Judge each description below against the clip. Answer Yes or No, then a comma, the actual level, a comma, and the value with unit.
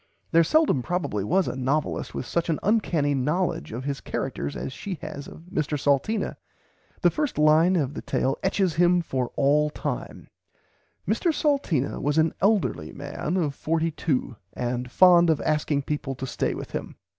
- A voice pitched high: No, medium, 150 Hz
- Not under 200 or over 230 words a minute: No, average, 170 wpm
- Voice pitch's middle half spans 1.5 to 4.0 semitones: No, average, 4.4 semitones